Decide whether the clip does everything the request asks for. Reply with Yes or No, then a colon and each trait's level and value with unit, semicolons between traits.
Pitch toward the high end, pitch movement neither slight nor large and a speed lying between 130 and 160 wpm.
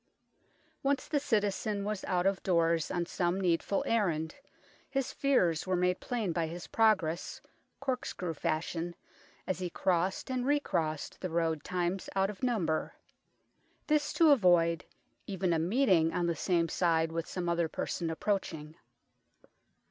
No: medium, 180 Hz; average, 3.9 semitones; average, 140 wpm